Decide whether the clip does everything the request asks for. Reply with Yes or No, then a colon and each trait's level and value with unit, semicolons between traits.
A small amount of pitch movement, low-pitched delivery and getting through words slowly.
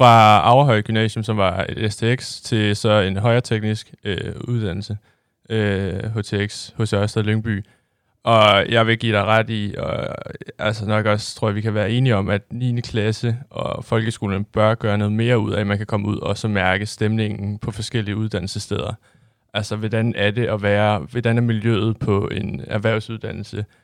No: narrow, 1.7 semitones; low, 110 Hz; average, 180 wpm